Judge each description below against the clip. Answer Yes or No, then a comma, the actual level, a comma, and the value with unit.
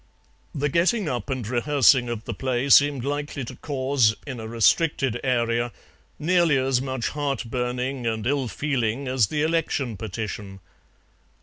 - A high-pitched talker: No, low, 130 Hz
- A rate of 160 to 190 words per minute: No, average, 145 wpm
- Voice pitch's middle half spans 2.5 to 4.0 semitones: Yes, average, 3.4 semitones